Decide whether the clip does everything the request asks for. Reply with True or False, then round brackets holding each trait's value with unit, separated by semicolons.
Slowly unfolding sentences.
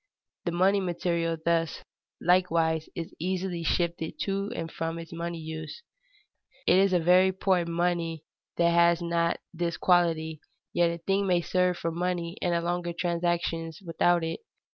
False (150 wpm)